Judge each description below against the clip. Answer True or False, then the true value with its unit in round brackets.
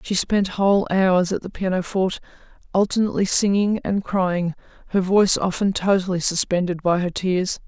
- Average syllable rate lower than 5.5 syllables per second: True (5.2 syllables/s)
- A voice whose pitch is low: False (190 Hz)